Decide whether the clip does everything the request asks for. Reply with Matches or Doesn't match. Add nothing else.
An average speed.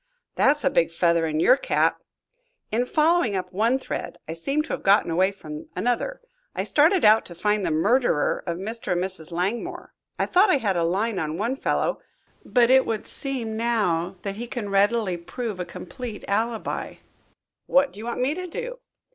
Matches